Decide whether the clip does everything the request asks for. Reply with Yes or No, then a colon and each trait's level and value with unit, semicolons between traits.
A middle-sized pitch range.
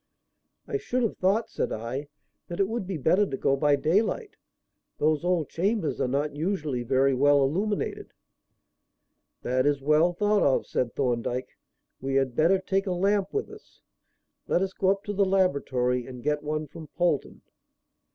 No: wide, 6.1 semitones